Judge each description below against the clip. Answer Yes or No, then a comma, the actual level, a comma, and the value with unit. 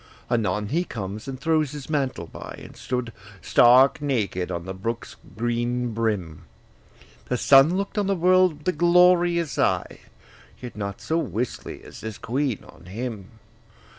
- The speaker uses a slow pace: No, average, 150 wpm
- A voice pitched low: Yes, low, 125 Hz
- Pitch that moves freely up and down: Yes, wide, 6.8 semitones